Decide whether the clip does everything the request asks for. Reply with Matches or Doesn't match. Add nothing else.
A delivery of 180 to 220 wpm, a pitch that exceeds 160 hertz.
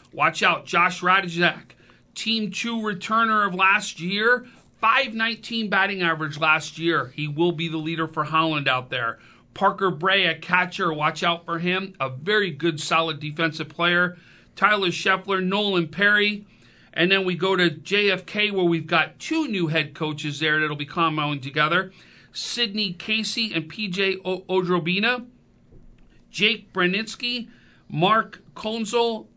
Doesn't match